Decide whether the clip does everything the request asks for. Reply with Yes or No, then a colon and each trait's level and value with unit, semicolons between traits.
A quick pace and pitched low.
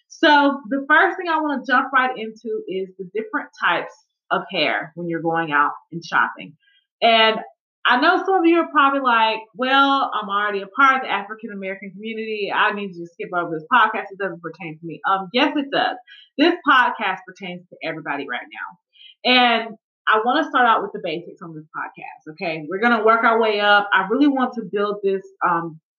No: fast, 210 wpm; high, 220 Hz